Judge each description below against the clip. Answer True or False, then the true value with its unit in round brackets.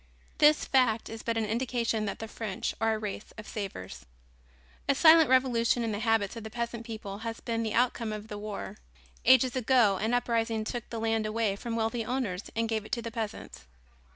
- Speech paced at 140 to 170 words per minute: False (205 wpm)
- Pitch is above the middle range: True (225 Hz)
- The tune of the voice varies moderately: False (1.9 semitones)